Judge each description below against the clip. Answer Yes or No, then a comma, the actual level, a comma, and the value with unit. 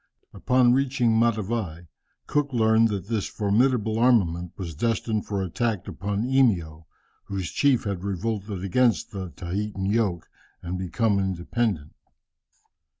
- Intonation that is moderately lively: Yes, average, 3.9 semitones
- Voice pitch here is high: No, low, 105 Hz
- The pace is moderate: No, slow, 125 wpm